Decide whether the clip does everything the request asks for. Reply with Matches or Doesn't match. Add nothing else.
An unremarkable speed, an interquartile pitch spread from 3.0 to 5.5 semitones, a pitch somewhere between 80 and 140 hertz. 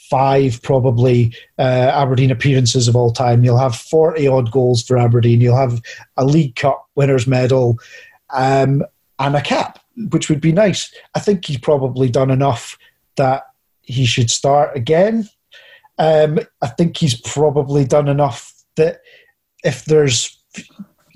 Matches